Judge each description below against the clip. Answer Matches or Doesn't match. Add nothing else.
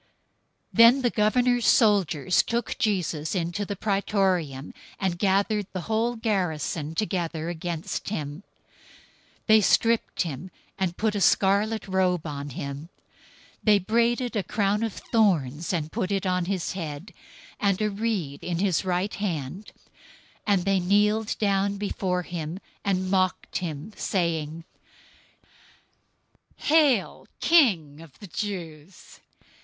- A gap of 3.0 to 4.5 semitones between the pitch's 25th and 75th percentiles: Matches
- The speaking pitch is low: Doesn't match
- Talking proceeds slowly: Matches